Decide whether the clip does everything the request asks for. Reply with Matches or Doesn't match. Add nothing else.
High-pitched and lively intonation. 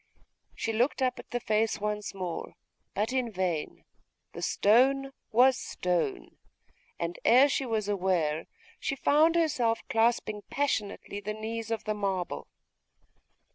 Doesn't match